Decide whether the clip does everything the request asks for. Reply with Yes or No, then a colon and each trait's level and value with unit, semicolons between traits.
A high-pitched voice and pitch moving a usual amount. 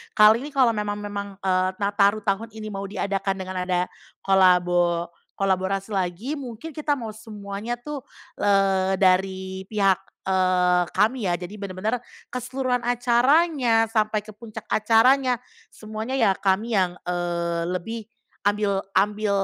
Yes: high, 205 Hz; average, 3.2 semitones